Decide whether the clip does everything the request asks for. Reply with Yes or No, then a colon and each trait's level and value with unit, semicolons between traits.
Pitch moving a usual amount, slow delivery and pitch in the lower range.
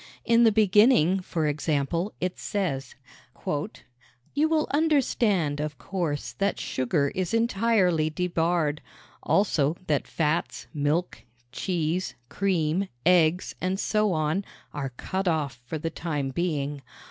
No: average, 4.6 semitones; slow, 120 wpm; medium, 170 Hz